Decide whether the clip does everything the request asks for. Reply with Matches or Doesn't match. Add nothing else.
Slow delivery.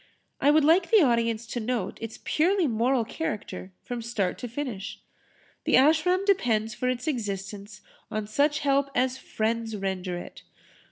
Doesn't match